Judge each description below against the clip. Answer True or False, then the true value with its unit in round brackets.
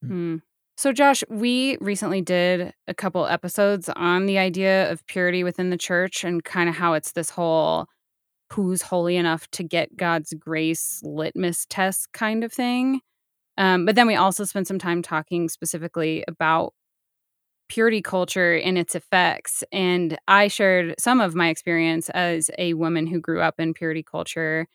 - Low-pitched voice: False (180 Hz)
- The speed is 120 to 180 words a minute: True (165 wpm)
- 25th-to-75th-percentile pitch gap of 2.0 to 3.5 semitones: True (2.6 semitones)